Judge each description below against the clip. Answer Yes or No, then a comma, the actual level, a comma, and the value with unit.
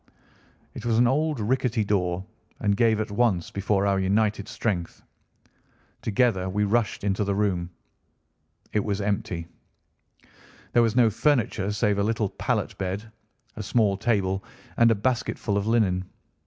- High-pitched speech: No, low, 105 Hz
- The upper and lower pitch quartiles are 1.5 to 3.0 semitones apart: Yes, narrow, 2.6 semitones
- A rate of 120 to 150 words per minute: Yes, average, 145 wpm